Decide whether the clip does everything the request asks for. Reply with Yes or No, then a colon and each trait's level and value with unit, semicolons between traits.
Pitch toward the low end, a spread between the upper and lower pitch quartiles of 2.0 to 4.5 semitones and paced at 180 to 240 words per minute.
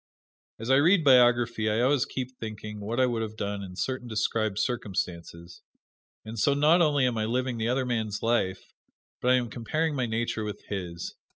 Yes: low, 115 Hz; average, 3.2 semitones; average, 190 wpm